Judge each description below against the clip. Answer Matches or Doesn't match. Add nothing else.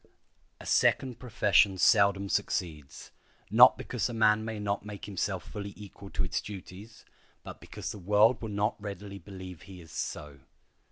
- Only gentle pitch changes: Matches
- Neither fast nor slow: Matches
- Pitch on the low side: Matches